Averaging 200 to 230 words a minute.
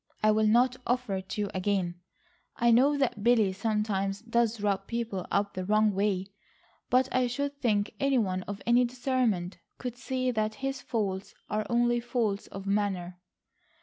No: average, 170 wpm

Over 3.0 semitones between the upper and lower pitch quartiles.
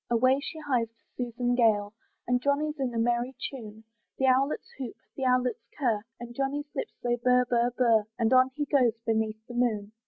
No: narrow, 2.4 semitones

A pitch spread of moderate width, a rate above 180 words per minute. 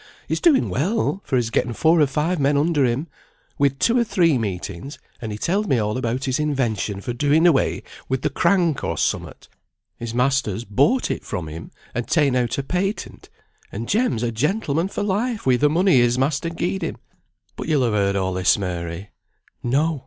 No: wide, 6.3 semitones; average, 195 wpm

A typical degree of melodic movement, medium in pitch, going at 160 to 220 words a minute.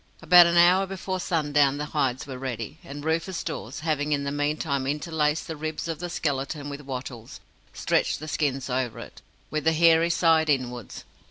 Yes: average, 3.2 semitones; medium, 150 Hz; average, 180 wpm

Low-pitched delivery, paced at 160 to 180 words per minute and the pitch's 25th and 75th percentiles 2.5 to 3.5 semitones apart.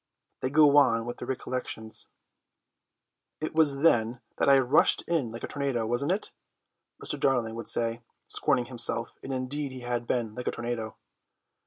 Yes: low, 125 Hz; average, 165 wpm; average, 3.1 semitones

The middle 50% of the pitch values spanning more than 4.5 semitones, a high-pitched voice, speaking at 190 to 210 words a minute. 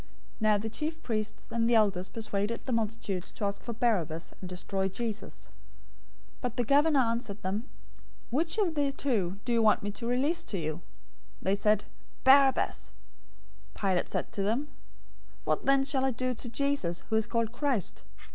No: average, 4.9 semitones; high, 230 Hz; average, 180 wpm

